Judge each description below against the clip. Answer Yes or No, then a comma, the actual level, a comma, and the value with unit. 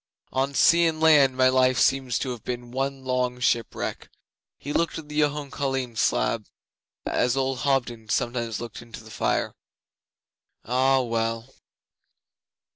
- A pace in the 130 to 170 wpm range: Yes, average, 140 wpm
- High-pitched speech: No, low, 130 Hz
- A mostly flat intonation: Yes, narrow, 2.3 semitones